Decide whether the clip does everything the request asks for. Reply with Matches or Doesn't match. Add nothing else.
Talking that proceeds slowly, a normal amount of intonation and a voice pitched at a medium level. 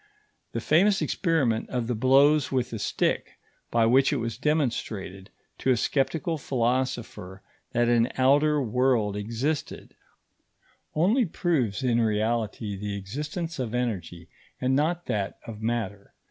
Doesn't match